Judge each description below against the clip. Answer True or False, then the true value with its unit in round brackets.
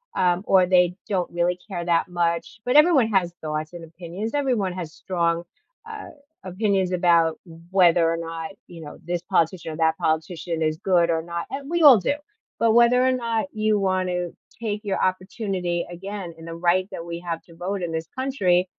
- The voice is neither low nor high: True (180 Hz)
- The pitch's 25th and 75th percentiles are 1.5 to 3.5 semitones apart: True (3.2 semitones)